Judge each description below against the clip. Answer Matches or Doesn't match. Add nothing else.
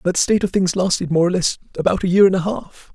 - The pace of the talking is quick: Matches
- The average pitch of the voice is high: Doesn't match